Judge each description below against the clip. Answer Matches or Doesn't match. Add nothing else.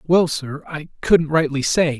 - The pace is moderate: Matches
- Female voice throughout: Doesn't match